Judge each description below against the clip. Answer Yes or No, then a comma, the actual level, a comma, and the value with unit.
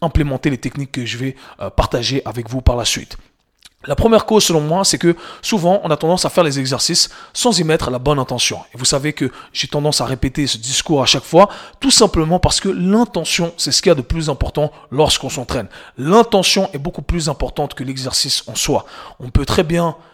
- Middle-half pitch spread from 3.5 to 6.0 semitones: Yes, average, 4.5 semitones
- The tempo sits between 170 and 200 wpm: No, fast, 220 wpm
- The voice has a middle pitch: Yes, medium, 150 Hz